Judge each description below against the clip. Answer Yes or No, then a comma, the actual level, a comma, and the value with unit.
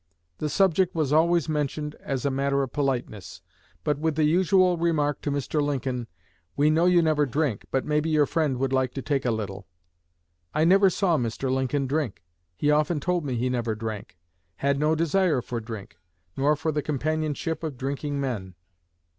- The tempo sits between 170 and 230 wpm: Yes, average, 180 wpm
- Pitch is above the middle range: No, medium, 145 Hz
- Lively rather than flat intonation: No, average, 3.5 semitones